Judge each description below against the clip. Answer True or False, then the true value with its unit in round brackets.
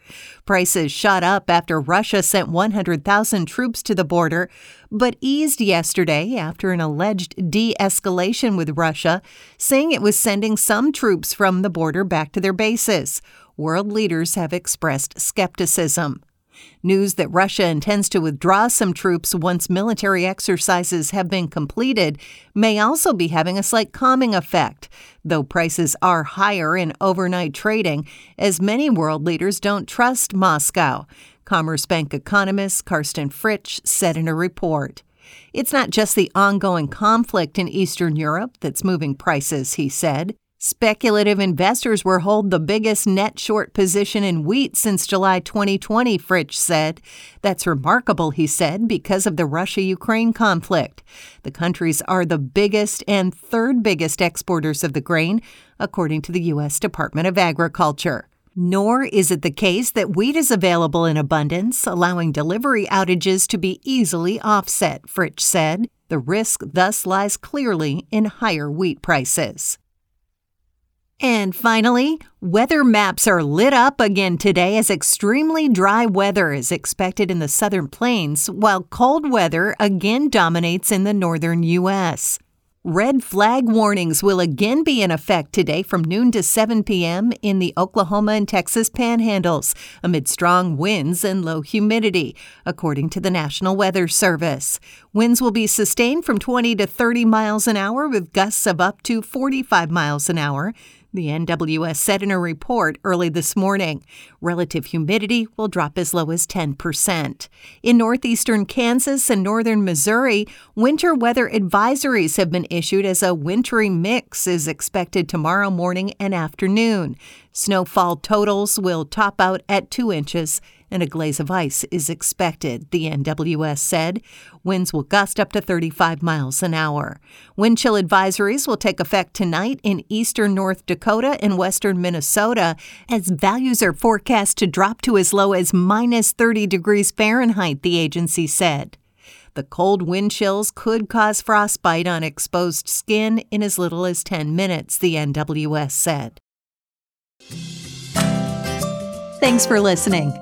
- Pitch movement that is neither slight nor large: True (4.0 semitones)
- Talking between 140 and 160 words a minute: True (150 wpm)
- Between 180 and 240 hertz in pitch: True (190 Hz)